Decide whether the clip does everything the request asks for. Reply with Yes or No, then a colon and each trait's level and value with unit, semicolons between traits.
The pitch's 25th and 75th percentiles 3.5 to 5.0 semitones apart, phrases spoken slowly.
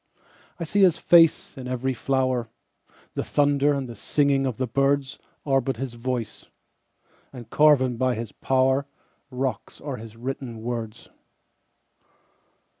No: narrow, 2.6 semitones; slow, 115 wpm